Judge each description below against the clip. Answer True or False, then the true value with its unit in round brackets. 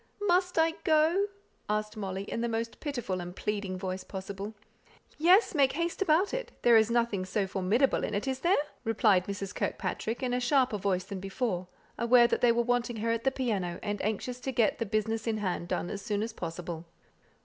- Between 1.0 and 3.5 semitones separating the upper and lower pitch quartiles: False (4.5 semitones)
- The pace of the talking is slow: False (200 wpm)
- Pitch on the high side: True (225 Hz)